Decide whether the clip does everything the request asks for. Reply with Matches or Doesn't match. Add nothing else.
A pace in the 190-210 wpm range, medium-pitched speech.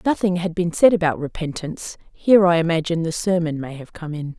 Matches